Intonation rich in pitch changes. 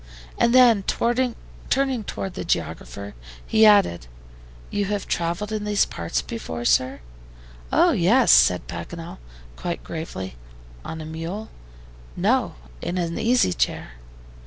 Yes: wide, 5.7 semitones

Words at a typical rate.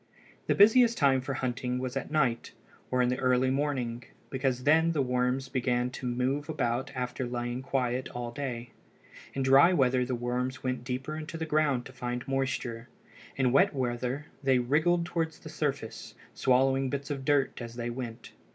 Yes: average, 175 wpm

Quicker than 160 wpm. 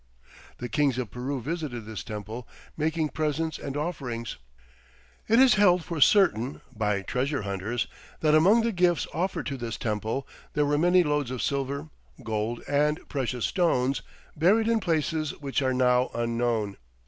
No: average, 155 wpm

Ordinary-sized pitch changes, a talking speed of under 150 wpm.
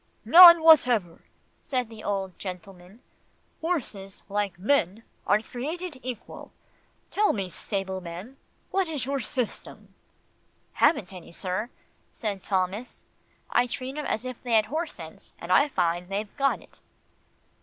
No: wide, 6.2 semitones; slow, 135 wpm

